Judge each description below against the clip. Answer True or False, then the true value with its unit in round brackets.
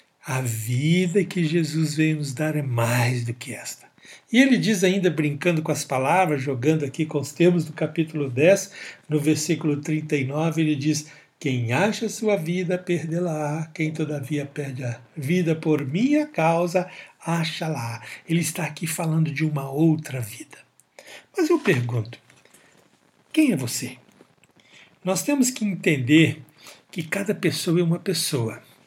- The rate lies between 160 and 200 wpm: False (150 wpm)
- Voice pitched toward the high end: False (155 Hz)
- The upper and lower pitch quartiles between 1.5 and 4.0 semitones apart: True (3.5 semitones)